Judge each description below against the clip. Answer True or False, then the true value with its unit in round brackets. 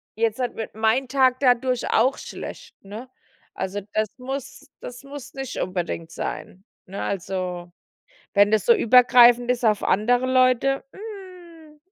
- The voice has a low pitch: False (245 Hz)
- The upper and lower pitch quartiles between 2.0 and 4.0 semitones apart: False (4.4 semitones)